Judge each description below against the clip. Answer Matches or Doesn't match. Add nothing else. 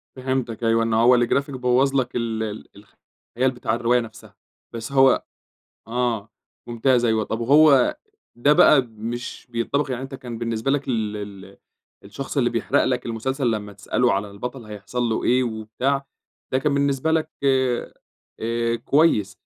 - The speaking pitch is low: Matches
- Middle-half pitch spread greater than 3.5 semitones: Doesn't match